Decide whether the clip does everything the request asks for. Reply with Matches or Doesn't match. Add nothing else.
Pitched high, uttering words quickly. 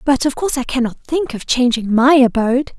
Matches